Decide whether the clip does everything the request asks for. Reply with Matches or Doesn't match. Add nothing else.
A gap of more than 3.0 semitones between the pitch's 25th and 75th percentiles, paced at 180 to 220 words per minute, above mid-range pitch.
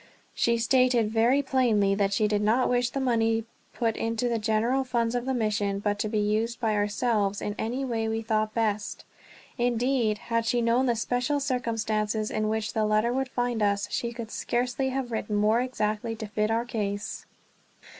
Doesn't match